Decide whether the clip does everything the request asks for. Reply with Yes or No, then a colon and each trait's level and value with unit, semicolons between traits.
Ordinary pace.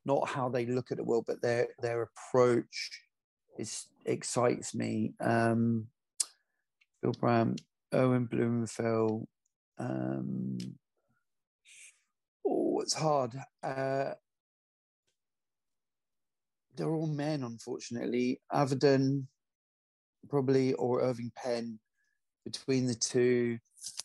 No: slow, 85 wpm